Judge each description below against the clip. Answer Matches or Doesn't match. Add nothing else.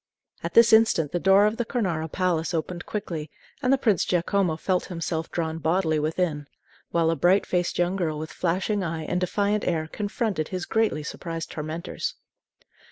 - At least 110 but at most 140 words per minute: Doesn't match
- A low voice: Doesn't match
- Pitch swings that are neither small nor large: Matches